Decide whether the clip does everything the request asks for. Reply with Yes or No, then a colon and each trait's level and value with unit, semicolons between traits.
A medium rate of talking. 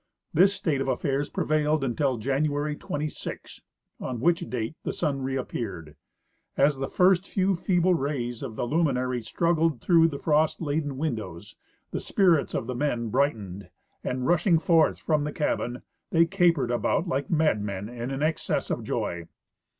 Yes: average, 160 wpm